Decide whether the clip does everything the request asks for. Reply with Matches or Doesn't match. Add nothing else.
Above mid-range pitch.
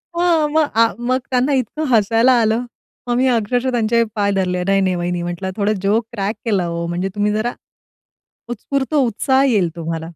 Matches